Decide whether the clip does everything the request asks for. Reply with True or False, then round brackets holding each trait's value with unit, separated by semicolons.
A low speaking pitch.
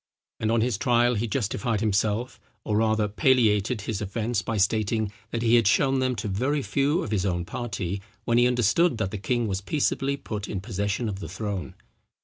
True (110 Hz)